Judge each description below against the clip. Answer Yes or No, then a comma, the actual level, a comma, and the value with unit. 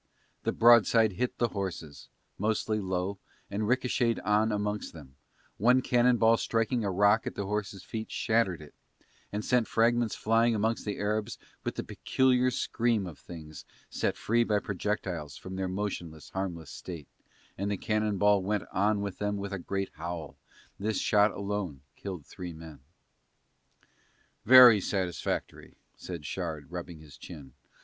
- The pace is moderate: Yes, average, 155 wpm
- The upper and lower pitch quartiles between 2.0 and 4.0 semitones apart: Yes, average, 3.7 semitones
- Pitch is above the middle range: No, low, 100 Hz